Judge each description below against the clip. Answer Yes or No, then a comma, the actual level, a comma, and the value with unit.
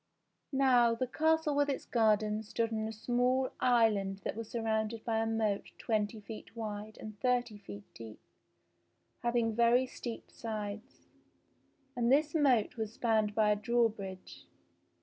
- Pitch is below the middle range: No, high, 225 Hz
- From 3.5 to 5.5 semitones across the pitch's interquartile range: No, narrow, 2.4 semitones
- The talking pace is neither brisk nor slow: Yes, average, 145 wpm